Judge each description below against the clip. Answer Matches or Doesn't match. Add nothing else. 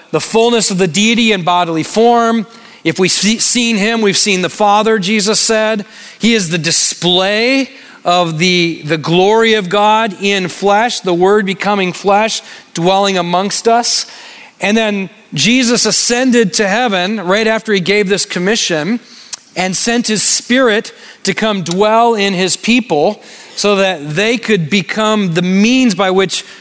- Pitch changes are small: Doesn't match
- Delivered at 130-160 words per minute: Matches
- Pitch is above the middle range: Matches